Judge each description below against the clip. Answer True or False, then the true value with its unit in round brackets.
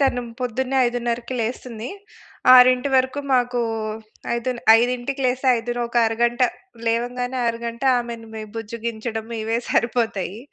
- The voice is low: False (240 Hz)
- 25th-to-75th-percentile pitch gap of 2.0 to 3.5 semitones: False (1.4 semitones)